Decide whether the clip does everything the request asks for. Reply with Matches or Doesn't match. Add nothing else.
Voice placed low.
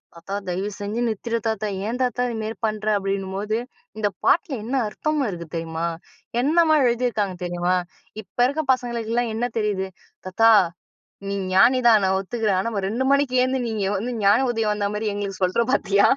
Doesn't match